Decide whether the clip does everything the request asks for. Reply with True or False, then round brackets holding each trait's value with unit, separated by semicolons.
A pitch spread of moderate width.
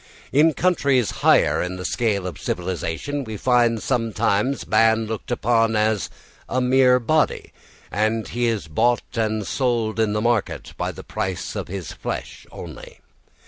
True (3.0 semitones)